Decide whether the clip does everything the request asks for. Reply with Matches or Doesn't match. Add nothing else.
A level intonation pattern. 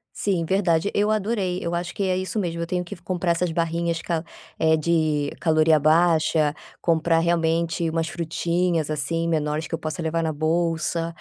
Matches